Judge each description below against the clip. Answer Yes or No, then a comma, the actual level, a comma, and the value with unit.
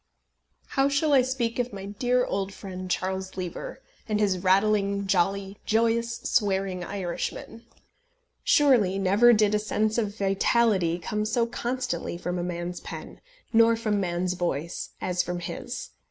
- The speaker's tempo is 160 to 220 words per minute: No, average, 145 wpm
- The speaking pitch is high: Yes, high, 200 Hz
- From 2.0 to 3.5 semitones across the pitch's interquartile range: No, average, 3.9 semitones